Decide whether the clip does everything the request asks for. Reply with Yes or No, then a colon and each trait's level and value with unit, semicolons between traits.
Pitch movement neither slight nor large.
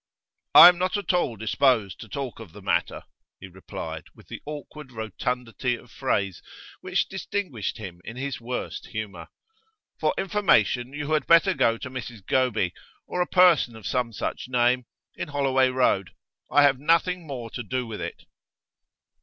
Yes: average, 4.8 semitones